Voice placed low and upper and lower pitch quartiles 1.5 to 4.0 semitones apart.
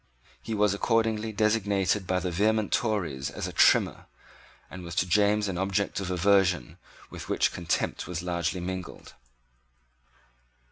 Yes: very low, 95 Hz; average, 2.9 semitones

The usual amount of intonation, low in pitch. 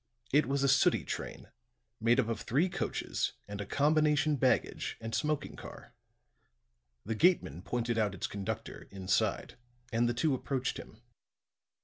Yes: average, 4.9 semitones; low, 120 Hz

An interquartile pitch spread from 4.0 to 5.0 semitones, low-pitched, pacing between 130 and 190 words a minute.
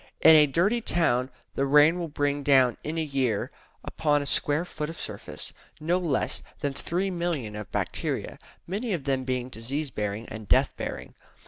No: average, 4.4 semitones; medium, 145 Hz; average, 175 wpm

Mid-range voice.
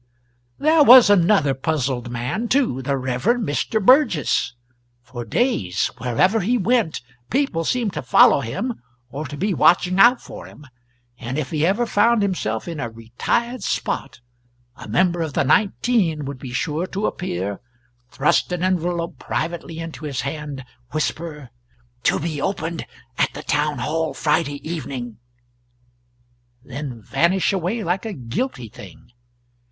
Yes: medium, 160 Hz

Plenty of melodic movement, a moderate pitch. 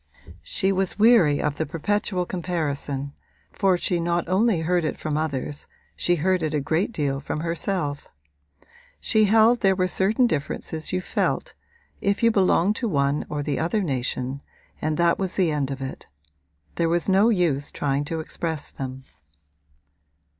No: average, 4.6 semitones; medium, 170 Hz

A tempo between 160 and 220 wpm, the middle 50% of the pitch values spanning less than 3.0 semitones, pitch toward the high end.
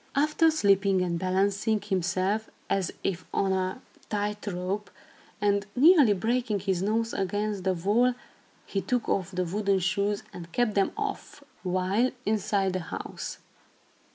No: average, 140 wpm; narrow, 2.6 semitones; high, 200 Hz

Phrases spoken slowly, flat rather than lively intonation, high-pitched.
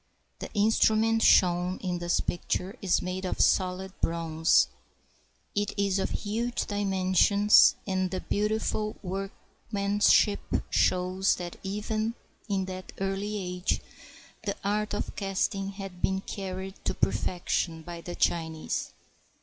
Yes: slow, 125 wpm; narrow, 2.1 semitones; high, 195 Hz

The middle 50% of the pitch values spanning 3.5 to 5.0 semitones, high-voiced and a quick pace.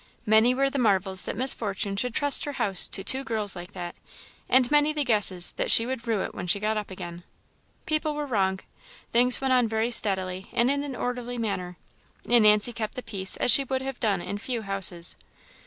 Yes: average, 4.5 semitones; high, 225 Hz; fast, 215 wpm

